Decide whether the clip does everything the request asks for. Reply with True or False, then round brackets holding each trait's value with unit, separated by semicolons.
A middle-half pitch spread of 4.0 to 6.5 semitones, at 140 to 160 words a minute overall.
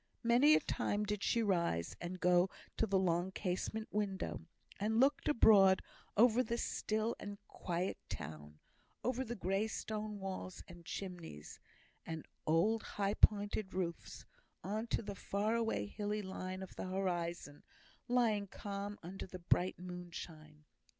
False (3.4 semitones; 145 wpm)